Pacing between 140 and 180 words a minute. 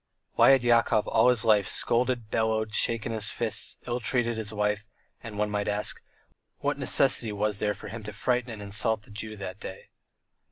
No: average, 190 wpm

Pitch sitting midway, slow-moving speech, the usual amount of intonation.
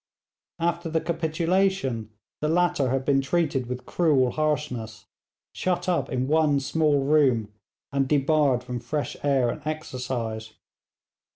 Yes: medium, 145 Hz; slow, 125 wpm; average, 4.1 semitones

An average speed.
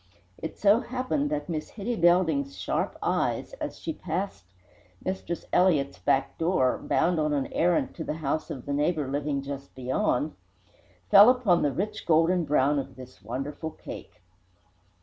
Yes: average, 155 wpm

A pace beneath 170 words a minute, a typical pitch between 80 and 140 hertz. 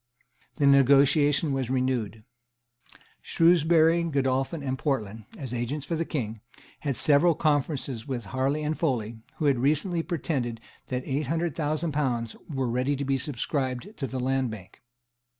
Yes: average, 150 wpm; low, 135 Hz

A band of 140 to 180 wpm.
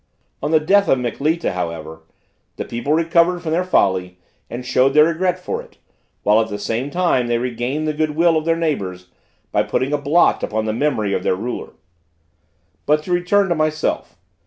No: average, 190 wpm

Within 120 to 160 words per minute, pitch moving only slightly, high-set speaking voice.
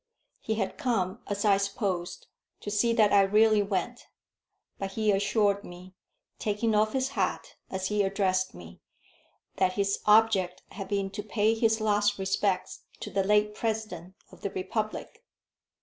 Yes: average, 155 wpm; narrow, 2.0 semitones; high, 205 Hz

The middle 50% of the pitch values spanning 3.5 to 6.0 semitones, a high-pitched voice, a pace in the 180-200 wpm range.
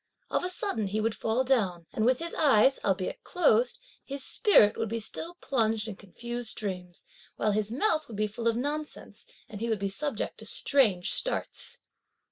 Yes: average, 4.8 semitones; high, 225 Hz; average, 185 wpm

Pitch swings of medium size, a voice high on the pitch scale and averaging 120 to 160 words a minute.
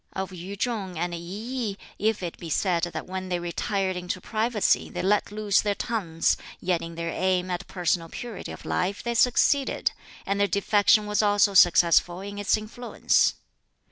No: average, 3.1 semitones; high, 195 Hz; average, 175 wpm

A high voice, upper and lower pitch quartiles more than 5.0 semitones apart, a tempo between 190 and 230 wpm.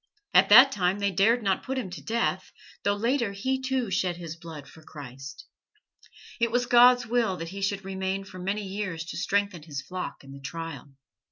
Yes: high, 195 Hz; wide, 5.6 semitones; average, 195 wpm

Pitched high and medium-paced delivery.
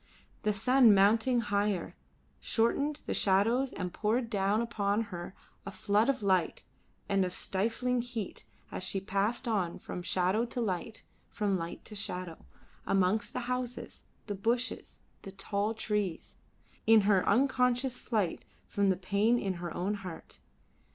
Yes: high, 205 Hz; average, 145 wpm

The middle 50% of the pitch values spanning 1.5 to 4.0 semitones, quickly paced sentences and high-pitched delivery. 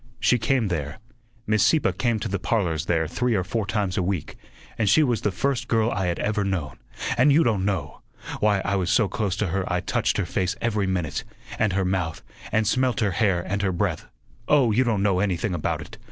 No: average, 3.6 semitones; fast, 225 wpm; low, 100 Hz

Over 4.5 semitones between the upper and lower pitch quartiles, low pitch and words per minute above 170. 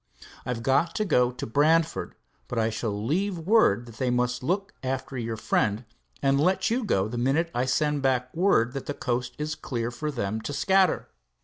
Yes: average, 5.1 semitones; low, 130 Hz; average, 195 wpm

